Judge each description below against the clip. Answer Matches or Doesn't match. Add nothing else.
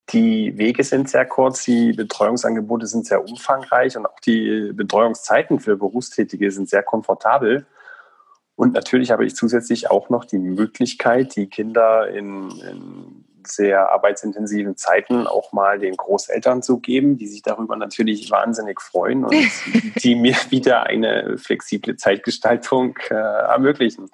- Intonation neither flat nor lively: Matches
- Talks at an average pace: Matches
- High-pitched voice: Doesn't match